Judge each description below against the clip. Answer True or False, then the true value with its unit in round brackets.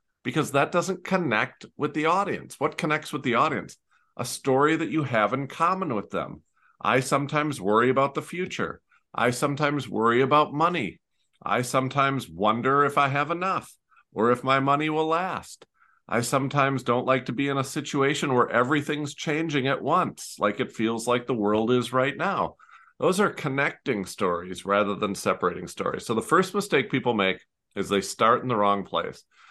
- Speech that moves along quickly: False (180 wpm)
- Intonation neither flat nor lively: True (3.7 semitones)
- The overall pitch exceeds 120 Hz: True (135 Hz)